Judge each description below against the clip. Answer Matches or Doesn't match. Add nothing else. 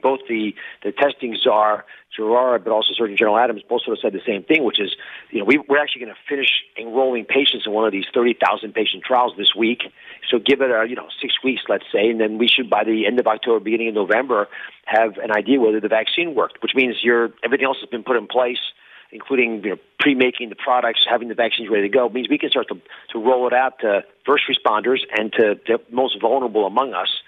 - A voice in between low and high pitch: Doesn't match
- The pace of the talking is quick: Matches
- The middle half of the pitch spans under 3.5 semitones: Matches